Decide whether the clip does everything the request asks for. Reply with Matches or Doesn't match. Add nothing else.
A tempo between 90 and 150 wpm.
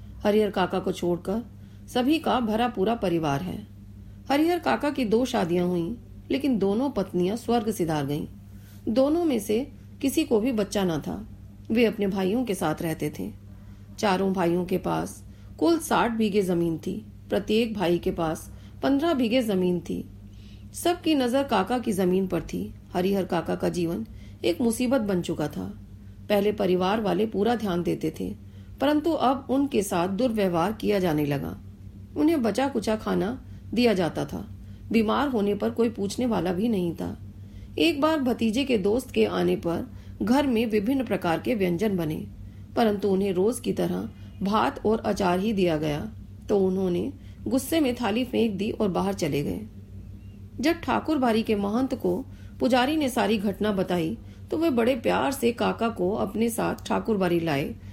Doesn't match